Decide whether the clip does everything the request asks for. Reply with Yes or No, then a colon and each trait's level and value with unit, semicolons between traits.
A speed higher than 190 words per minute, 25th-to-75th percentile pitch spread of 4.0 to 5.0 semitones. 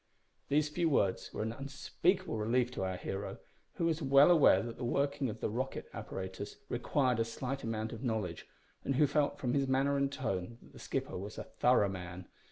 Yes: average, 200 wpm; average, 4.7 semitones